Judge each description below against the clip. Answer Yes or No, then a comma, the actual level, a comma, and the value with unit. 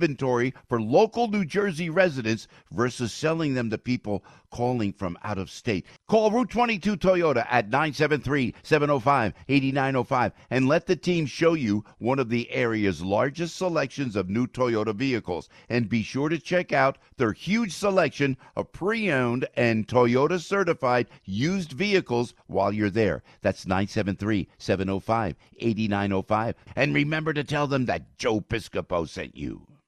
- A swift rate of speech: No, average, 140 wpm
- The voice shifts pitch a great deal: Yes, wide, 6.3 semitones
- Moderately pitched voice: No, low, 130 Hz